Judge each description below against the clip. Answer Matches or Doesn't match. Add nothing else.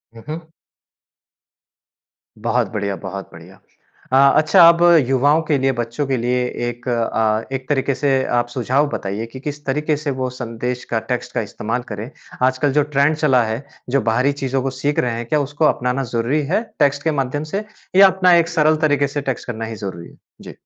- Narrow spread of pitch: Doesn't match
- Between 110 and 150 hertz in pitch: Matches